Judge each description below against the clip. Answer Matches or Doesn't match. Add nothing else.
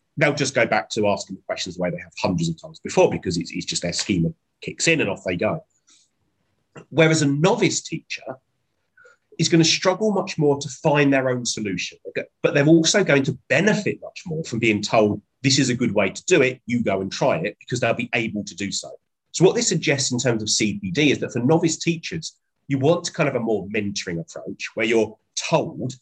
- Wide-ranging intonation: Matches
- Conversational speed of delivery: Doesn't match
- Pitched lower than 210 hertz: Matches